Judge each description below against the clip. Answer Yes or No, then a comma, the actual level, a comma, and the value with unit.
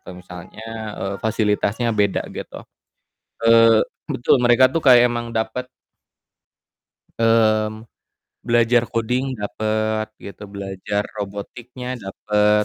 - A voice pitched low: Yes, low, 110 Hz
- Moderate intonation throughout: No, narrow, 2.3 semitones